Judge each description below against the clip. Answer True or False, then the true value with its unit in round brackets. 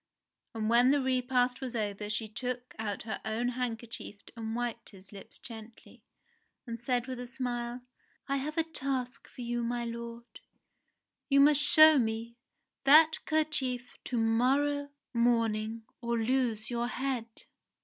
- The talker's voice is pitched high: True (240 Hz)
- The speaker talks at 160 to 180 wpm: False (145 wpm)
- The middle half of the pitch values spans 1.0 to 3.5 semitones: True (2.4 semitones)